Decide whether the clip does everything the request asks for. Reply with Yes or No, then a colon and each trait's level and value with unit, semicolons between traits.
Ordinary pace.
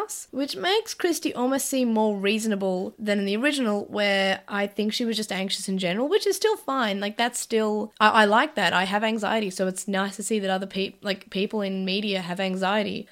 No: fast, 220 wpm